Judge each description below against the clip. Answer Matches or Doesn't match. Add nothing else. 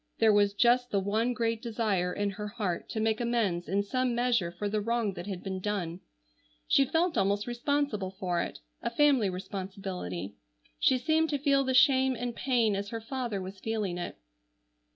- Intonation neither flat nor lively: Matches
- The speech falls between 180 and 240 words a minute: Matches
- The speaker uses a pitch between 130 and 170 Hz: Doesn't match